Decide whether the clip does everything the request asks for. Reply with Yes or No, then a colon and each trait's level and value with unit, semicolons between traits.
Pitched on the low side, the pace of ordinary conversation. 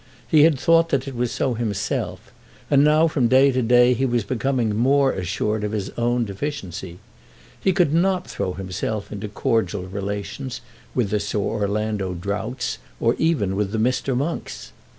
Yes: low, 120 Hz; average, 170 wpm